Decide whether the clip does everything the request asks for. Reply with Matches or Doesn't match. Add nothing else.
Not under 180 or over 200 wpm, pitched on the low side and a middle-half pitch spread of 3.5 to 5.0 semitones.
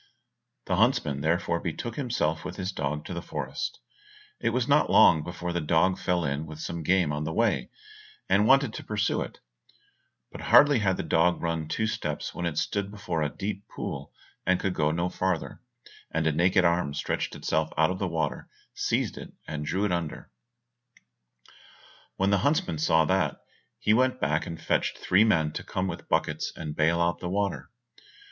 Matches